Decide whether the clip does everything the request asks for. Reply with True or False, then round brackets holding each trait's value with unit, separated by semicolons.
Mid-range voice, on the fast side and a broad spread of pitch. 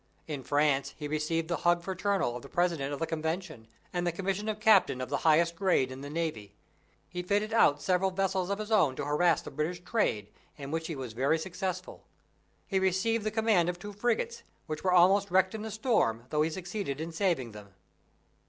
False (175 Hz; 210 wpm; 4.8 semitones)